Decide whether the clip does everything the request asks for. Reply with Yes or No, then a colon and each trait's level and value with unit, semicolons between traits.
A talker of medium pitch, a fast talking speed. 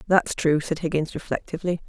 No: medium, 165 Hz; average, 160 wpm